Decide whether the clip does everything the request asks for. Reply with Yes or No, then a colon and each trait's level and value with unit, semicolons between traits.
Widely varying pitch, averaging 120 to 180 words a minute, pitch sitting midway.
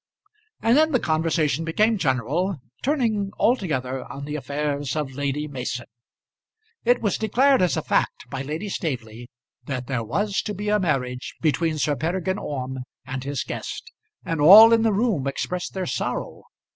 Yes: wide, 7.2 semitones; average, 160 wpm; medium, 155 Hz